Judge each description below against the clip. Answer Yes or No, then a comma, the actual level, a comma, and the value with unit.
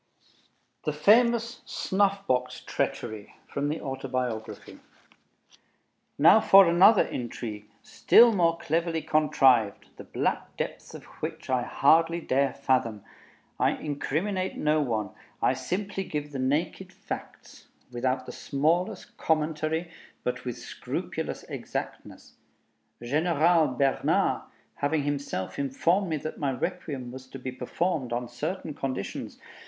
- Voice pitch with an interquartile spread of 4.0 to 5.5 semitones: Yes, average, 4.9 semitones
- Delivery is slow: Yes, slow, 120 wpm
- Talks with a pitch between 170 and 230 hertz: No, medium, 145 Hz